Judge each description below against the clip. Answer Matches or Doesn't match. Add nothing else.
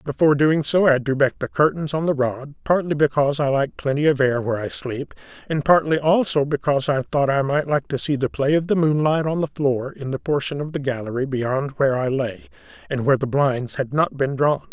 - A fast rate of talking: Matches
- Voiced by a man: Matches